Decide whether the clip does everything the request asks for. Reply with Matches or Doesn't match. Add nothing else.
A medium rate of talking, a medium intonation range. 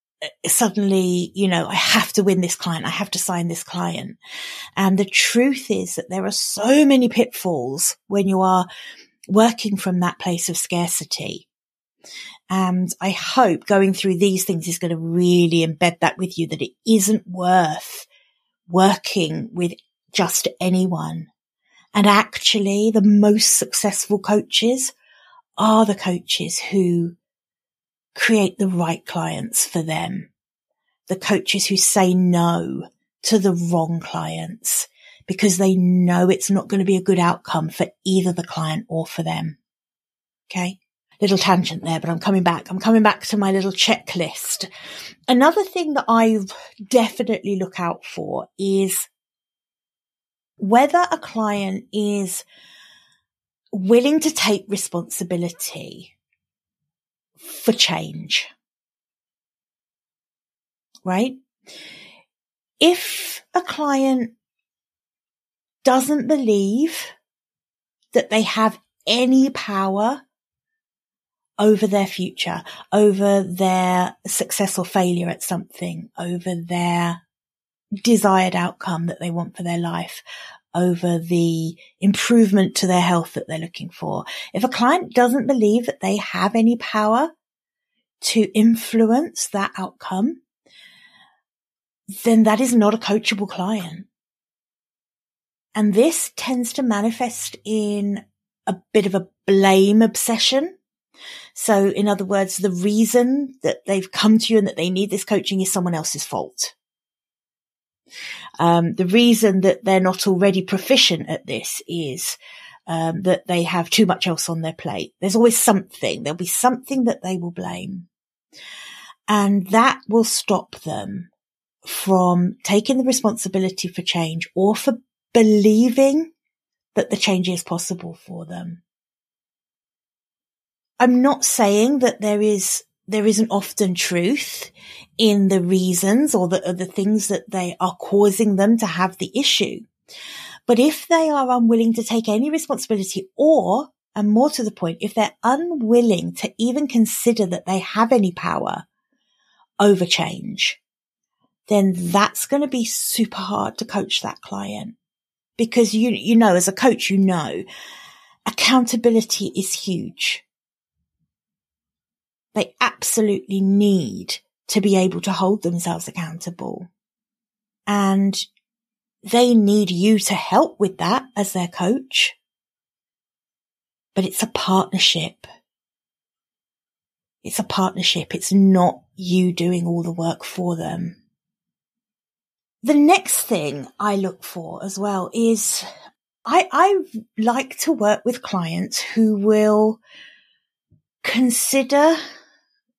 Doesn't match